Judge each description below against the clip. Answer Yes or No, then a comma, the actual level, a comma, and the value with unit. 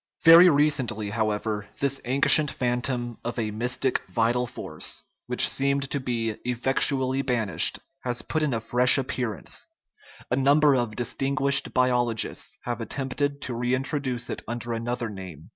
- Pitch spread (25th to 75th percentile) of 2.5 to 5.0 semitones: Yes, average, 2.8 semitones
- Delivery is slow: No, average, 145 wpm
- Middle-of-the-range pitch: No, low, 125 Hz